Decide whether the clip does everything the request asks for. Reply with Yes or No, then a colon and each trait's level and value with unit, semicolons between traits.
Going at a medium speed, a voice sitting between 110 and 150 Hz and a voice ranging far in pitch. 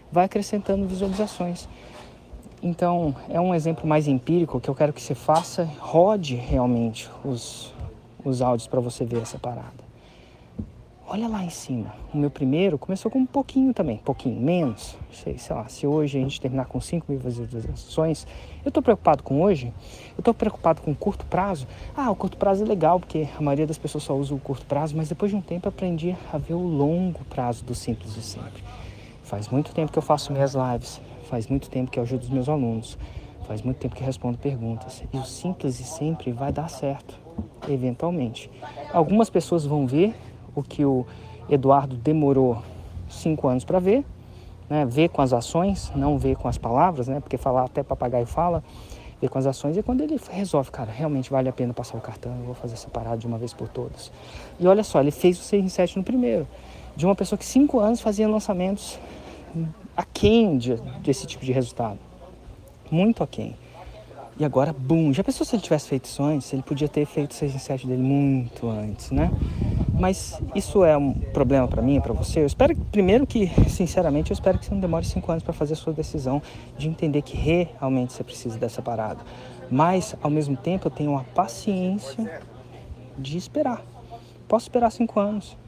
No: fast, 195 wpm; medium, 140 Hz; wide, 5.9 semitones